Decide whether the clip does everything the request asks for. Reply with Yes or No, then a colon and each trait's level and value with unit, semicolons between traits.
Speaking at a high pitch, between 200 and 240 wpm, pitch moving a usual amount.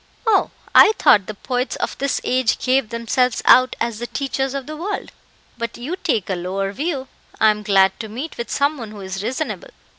Yes: high, 245 Hz; fast, 205 wpm; average, 4.7 semitones